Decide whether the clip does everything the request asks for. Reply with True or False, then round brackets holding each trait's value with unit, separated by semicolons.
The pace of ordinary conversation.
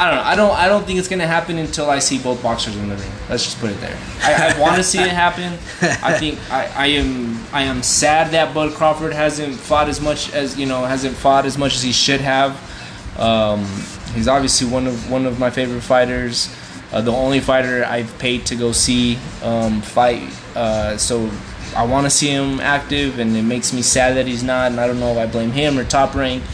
False (235 wpm)